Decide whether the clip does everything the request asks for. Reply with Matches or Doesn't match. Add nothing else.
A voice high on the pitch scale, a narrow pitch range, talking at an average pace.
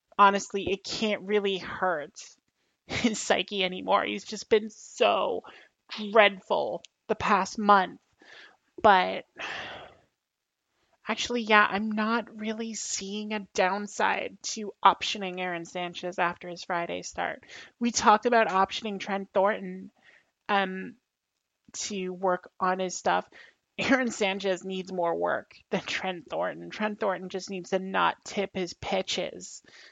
Doesn't match